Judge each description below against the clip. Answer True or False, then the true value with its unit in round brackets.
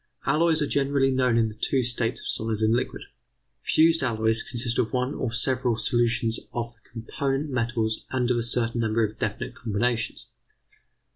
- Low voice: True (120 Hz)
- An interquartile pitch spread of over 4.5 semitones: False (2.4 semitones)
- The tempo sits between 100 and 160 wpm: False (170 wpm)